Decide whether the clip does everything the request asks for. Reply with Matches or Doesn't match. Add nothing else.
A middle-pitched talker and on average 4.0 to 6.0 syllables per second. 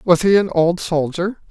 Matches